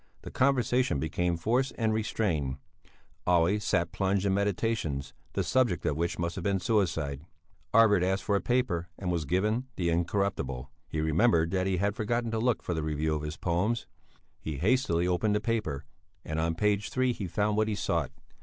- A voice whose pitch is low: Yes, very low, 95 Hz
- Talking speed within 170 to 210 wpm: Yes, average, 185 wpm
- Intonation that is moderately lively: Yes, average, 4.7 semitones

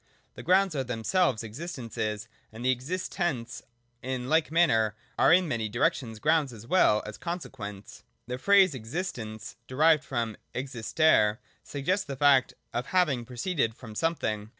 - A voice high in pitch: No, low, 130 Hz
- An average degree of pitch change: No, wide, 6.6 semitones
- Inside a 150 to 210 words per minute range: No, average, 140 wpm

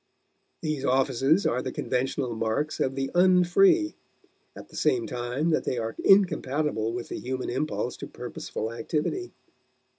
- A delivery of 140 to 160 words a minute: Yes, average, 150 wpm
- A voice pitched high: No, low, 135 Hz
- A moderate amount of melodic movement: No, wide, 5.9 semitones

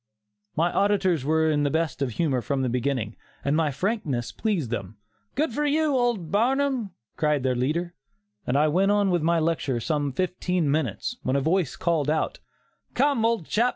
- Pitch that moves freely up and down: Yes, wide, 6.6 semitones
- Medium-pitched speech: Yes, medium, 160 Hz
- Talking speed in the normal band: Yes, average, 190 wpm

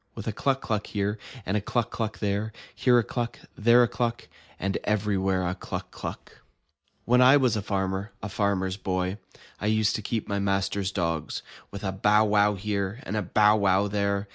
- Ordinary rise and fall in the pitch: No, narrow, 2.1 semitones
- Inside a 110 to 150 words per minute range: No, average, 195 wpm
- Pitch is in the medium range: No, low, 105 Hz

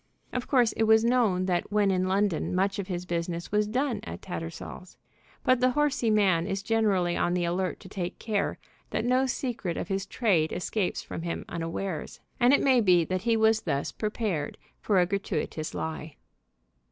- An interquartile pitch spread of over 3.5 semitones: Yes, average, 4.1 semitones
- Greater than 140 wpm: Yes, average, 185 wpm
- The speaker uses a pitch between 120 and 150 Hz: No, high, 195 Hz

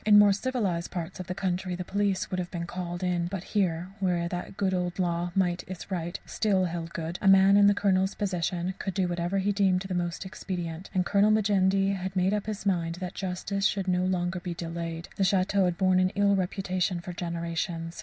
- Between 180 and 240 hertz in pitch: Yes, medium, 185 Hz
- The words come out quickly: Yes, fast, 215 wpm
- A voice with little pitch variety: Yes, narrow, 2.0 semitones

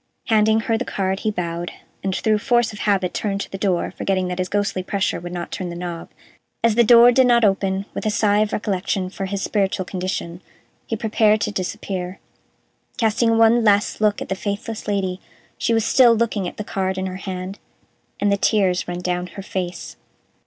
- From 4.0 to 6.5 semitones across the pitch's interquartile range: No, average, 2.7 semitones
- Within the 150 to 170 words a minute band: No, average, 200 wpm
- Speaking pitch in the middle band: No, high, 200 Hz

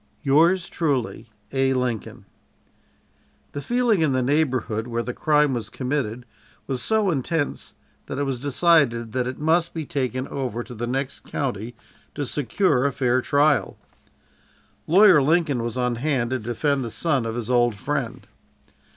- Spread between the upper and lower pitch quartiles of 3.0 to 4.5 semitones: Yes, average, 3.7 semitones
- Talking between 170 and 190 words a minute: No, average, 155 wpm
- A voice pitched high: No, low, 135 Hz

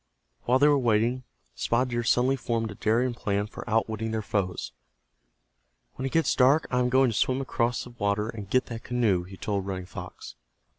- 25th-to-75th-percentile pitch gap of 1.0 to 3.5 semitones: Yes, average, 3.1 semitones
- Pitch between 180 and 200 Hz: No, low, 115 Hz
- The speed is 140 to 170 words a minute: No, average, 195 wpm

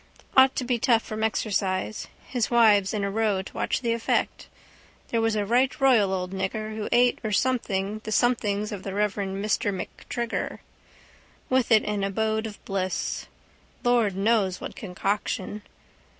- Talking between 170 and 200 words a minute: No, average, 160 wpm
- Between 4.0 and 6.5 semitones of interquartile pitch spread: No, average, 2.8 semitones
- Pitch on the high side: Yes, high, 215 Hz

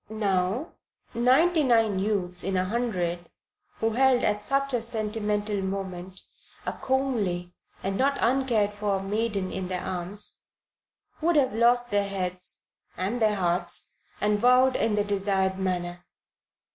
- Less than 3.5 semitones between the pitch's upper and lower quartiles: No, average, 4.2 semitones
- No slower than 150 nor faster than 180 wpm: No, slow, 135 wpm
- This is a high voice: Yes, high, 210 Hz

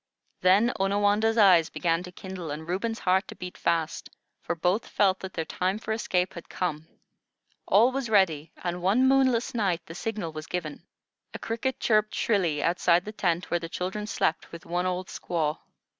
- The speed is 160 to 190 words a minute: Yes, average, 180 wpm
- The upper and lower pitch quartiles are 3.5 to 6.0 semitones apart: Yes, average, 3.8 semitones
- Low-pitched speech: No, medium, 185 Hz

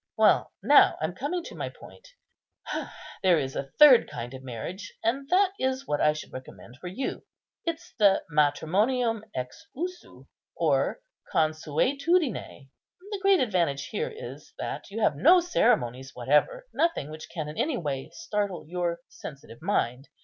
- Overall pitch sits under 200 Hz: Yes, medium, 185 Hz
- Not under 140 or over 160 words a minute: Yes, average, 150 wpm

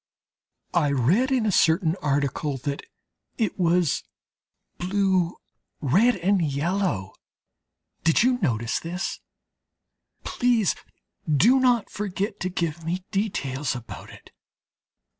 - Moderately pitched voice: Yes, medium, 175 Hz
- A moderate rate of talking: No, slow, 105 wpm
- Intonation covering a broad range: Yes, wide, 5.7 semitones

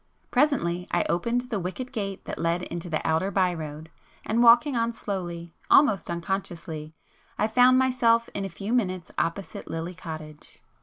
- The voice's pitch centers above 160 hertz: Yes, high, 190 Hz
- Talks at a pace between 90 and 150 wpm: No, average, 160 wpm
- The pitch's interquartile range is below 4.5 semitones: No, wide, 5.6 semitones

